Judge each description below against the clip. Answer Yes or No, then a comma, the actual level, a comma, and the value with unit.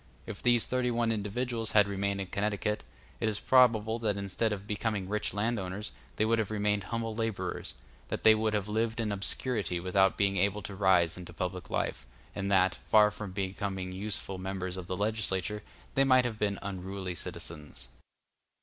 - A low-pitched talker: Yes, low, 105 Hz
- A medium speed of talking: Yes, average, 175 wpm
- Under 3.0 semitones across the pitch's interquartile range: Yes, narrow, 2.6 semitones